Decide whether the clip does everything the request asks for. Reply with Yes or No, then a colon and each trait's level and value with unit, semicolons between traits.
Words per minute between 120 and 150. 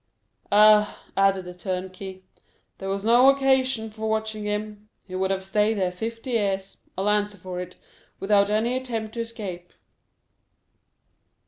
Yes: average, 140 wpm